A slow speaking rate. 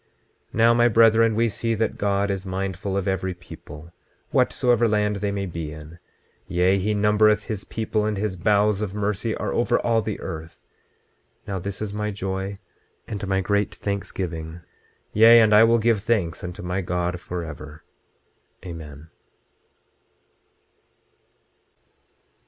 No: average, 145 wpm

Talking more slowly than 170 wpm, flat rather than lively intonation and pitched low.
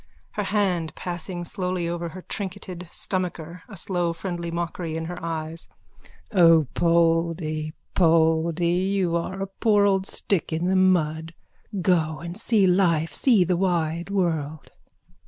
No: slow, 135 wpm; narrow, 2.3 semitones; medium, 175 Hz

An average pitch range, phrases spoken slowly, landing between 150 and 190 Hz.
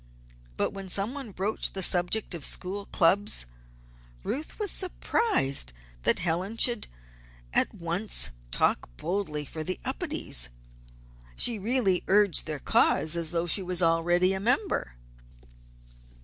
Yes: average, 4.6 semitones; slow, 125 wpm; medium, 185 Hz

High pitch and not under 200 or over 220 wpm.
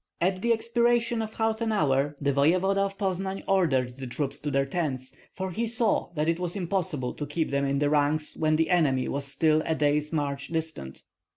No: medium, 160 Hz; fast, 205 wpm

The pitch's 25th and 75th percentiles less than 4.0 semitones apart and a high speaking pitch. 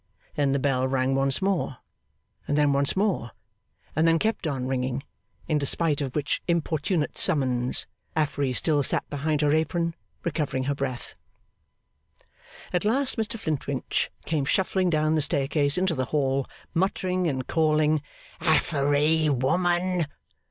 No: average, 3.5 semitones; medium, 150 Hz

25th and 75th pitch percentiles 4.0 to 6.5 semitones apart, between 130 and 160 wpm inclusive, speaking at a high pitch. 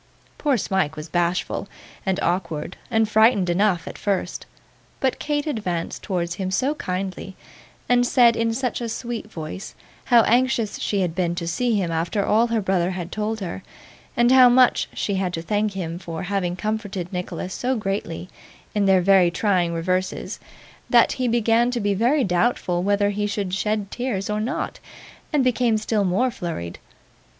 No: average, 4.3 semitones; average, 170 wpm; high, 200 Hz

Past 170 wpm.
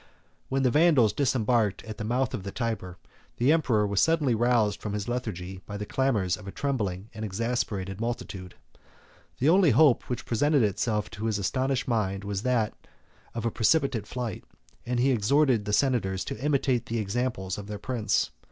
Yes: average, 180 wpm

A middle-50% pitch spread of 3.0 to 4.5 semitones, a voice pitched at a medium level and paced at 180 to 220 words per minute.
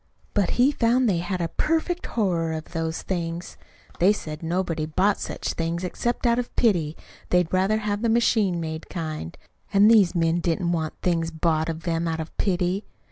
Yes: average, 4.0 semitones; medium, 175 Hz; average, 185 wpm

